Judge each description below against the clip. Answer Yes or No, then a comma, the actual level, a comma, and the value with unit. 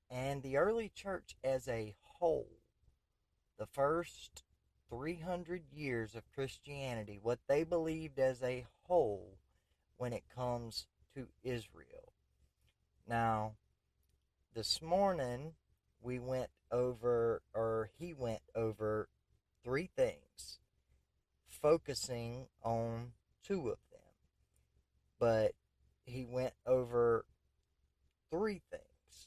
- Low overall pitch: Yes, low, 120 Hz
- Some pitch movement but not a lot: No, wide, 5.8 semitones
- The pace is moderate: No, slow, 95 wpm